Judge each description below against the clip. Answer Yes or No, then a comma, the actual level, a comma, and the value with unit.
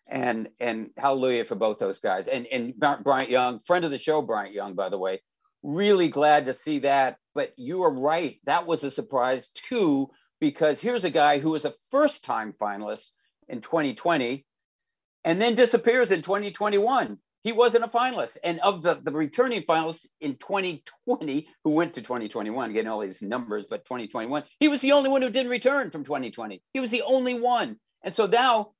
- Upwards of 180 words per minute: Yes, average, 190 wpm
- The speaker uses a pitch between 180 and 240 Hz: Yes, high, 190 Hz